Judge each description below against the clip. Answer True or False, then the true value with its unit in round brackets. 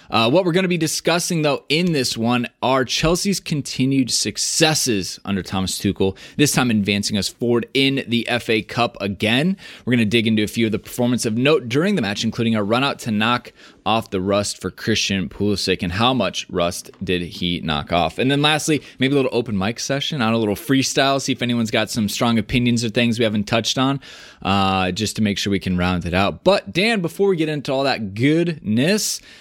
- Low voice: True (120 Hz)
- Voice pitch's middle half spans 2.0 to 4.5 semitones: False (5.3 semitones)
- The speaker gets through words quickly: True (220 wpm)